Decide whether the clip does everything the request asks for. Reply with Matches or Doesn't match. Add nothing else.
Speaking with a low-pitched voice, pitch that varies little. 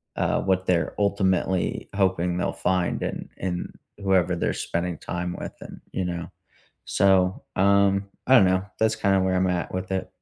Matches